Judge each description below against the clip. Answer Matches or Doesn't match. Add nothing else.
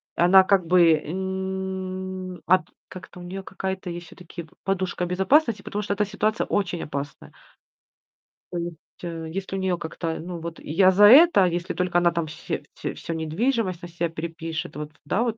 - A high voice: Doesn't match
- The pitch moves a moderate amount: Doesn't match